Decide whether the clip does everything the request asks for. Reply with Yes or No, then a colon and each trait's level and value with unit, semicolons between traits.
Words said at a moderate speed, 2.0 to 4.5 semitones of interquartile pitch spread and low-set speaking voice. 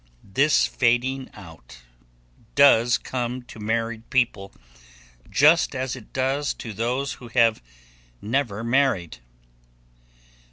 No: slow, 105 wpm; average, 3.0 semitones; low, 120 Hz